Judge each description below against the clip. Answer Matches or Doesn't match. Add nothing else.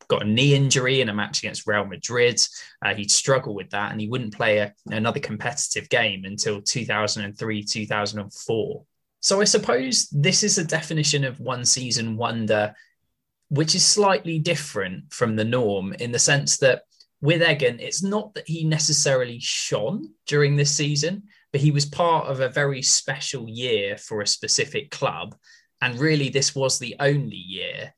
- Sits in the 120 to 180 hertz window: Matches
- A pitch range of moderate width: Doesn't match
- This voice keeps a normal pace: Matches